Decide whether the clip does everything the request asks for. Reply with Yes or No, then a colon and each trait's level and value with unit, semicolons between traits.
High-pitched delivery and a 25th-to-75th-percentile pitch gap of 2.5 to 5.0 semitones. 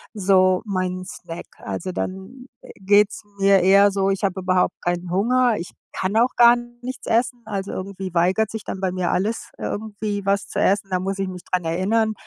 Yes: high, 195 Hz; average, 2.8 semitones